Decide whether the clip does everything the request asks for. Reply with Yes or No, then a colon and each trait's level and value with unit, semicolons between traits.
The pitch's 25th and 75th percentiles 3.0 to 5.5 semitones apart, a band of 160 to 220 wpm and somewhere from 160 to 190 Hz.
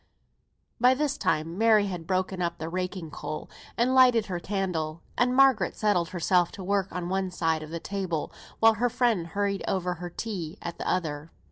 Yes: average, 3.8 semitones; average, 195 wpm; medium, 185 Hz